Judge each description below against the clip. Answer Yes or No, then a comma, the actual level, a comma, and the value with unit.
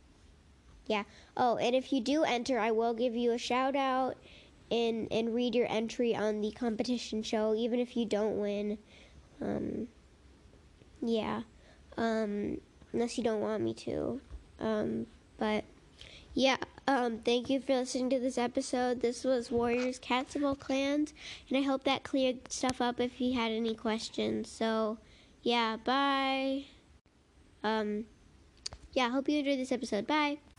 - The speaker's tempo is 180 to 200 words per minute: No, average, 155 wpm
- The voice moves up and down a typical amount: Yes, average, 3.1 semitones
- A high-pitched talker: Yes, high, 240 Hz